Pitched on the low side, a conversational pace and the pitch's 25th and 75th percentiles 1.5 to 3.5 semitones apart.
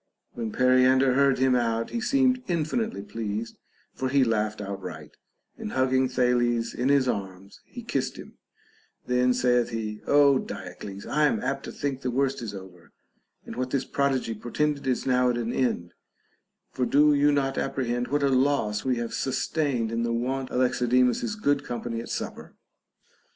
Yes: low, 125 Hz; average, 170 wpm; average, 3.1 semitones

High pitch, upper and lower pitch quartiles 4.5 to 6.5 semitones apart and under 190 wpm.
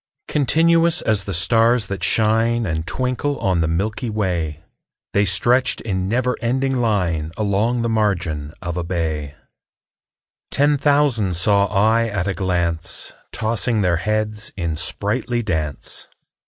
No: low, 105 Hz; average, 5.1 semitones; slow, 135 wpm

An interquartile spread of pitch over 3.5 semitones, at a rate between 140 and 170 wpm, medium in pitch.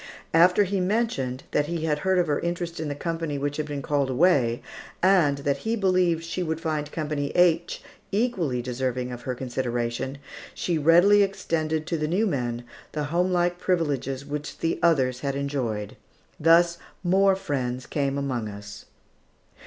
Yes: average, 4.6 semitones; average, 160 wpm; medium, 150 Hz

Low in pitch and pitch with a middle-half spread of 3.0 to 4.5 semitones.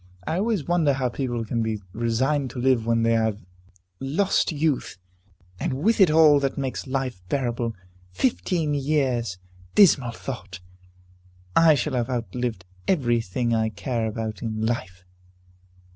Yes: low, 125 Hz; average, 4.1 semitones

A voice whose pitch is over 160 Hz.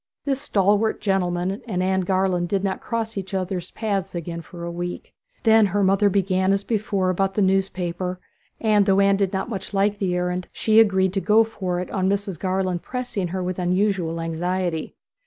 Yes: high, 190 Hz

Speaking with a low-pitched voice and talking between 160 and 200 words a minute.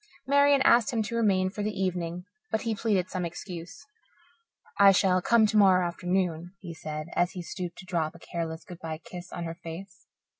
No: medium, 185 Hz; average, 190 wpm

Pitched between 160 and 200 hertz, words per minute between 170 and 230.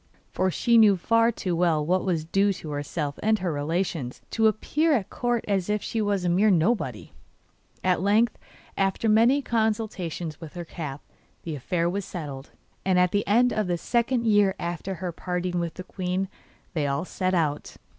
Yes: medium, 185 Hz; average, 185 wpm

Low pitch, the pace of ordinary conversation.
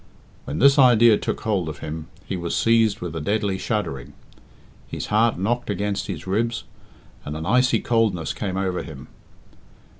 Yes: low, 100 Hz; average, 160 wpm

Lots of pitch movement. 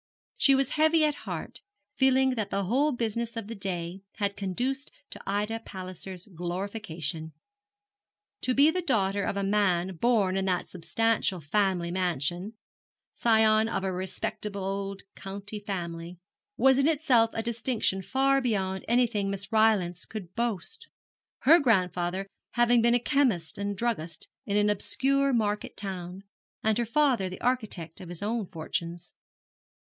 No: average, 4.4 semitones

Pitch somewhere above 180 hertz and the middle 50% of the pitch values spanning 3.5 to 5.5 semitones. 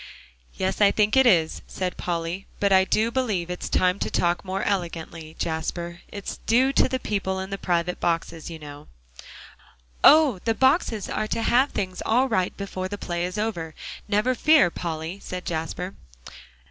Yes: high, 190 Hz; average, 3.9 semitones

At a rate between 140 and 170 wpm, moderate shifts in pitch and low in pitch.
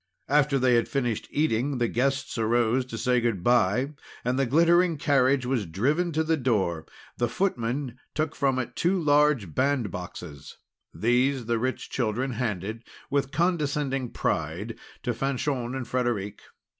Yes: average, 145 wpm; average, 3.6 semitones; low, 125 Hz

